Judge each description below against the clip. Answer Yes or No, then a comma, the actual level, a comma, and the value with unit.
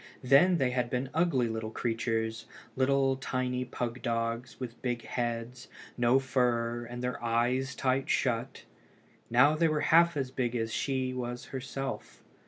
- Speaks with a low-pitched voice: Yes, low, 125 Hz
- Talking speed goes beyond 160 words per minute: No, average, 150 wpm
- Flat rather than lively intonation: Yes, narrow, 2.0 semitones